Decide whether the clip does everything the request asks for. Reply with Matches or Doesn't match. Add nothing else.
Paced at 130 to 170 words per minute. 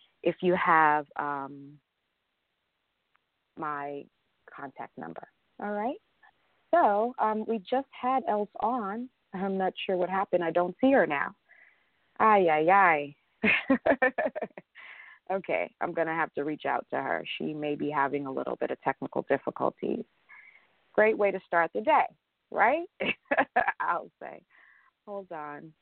Matches